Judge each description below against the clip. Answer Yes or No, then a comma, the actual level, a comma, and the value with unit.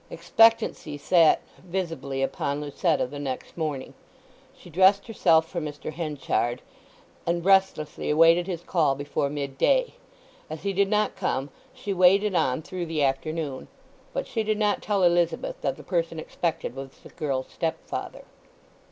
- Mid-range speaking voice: Yes, medium, 165 Hz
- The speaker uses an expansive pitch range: No, average, 4.6 semitones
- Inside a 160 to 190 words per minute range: No, average, 150 wpm